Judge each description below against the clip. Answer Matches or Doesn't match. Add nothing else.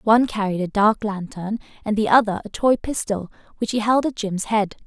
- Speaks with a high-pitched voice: Matches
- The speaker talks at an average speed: Doesn't match